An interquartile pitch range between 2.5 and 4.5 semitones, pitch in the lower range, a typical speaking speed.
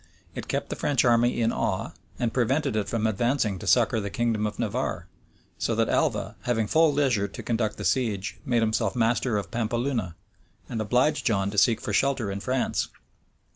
Yes: average, 2.9 semitones; low, 115 Hz; average, 185 wpm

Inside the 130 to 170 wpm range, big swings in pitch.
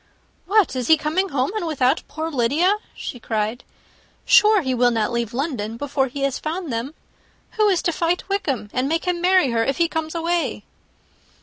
No: average, 190 wpm; wide, 5.7 semitones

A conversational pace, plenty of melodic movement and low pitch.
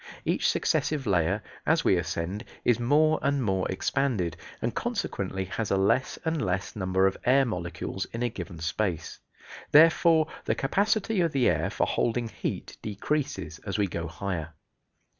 Yes: average, 160 wpm; wide, 7.1 semitones; low, 105 Hz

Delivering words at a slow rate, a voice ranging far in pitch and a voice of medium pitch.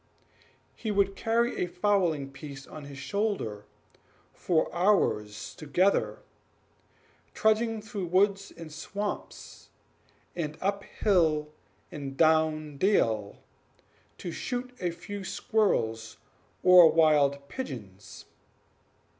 Yes: slow, 95 wpm; wide, 6.2 semitones; medium, 170 Hz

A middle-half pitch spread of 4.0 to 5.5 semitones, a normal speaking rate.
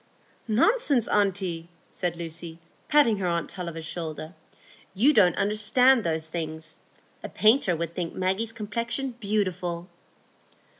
No: average, 4.8 semitones; slow, 115 wpm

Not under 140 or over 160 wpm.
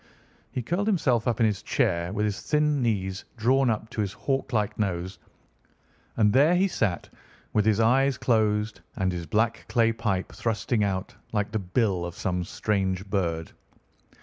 No: average, 170 wpm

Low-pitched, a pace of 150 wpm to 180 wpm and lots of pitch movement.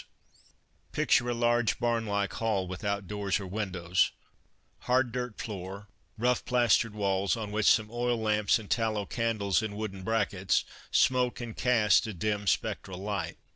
No: low, 105 Hz; average, 160 wpm; average, 2.8 semitones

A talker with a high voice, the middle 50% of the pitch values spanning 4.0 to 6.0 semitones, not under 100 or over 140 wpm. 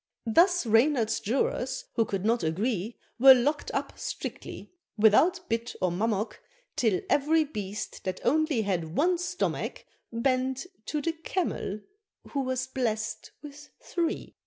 Yes: very high, 250 Hz; wide, 5.5 semitones; slow, 135 wpm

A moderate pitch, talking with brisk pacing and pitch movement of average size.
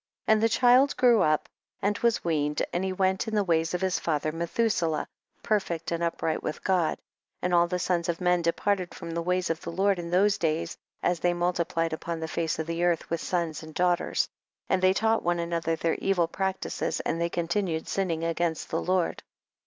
No: medium, 175 Hz; fast, 215 wpm; narrow, 2.2 semitones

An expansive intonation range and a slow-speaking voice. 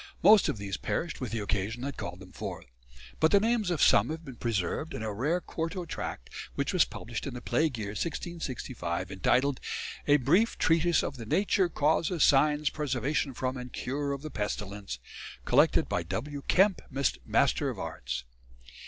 No: wide, 7.1 semitones; average, 175 wpm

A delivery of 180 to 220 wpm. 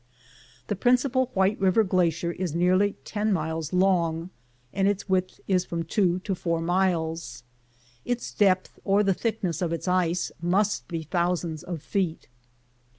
No: average, 150 wpm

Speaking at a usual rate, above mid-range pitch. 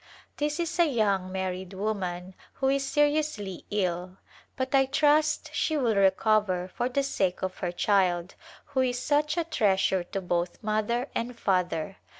Yes: average, 160 wpm; high, 210 Hz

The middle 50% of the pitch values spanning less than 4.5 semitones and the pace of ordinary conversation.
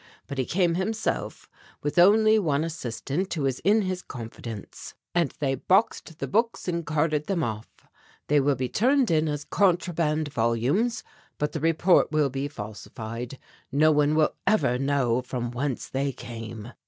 No: wide, 5.5 semitones; average, 160 wpm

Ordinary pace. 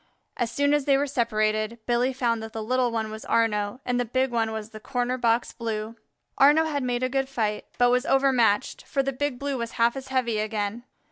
No: fast, 220 wpm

